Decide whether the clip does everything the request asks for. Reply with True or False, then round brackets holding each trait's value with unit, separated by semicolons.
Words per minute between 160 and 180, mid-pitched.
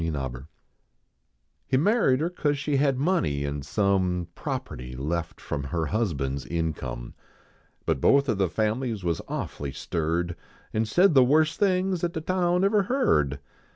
False (165 wpm; 110 Hz)